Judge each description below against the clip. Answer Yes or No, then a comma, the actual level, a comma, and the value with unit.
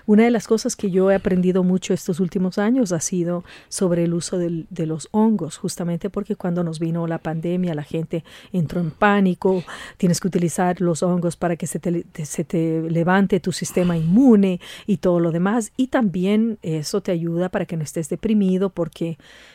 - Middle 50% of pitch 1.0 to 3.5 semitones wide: Yes, average, 2.7 semitones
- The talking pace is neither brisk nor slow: Yes, average, 195 wpm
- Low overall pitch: No, medium, 180 Hz